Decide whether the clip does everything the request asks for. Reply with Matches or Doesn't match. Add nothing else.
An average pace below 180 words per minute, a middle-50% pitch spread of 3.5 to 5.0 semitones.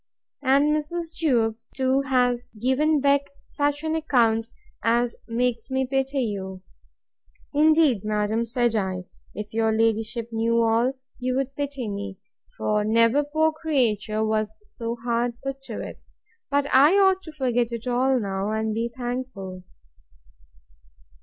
Matches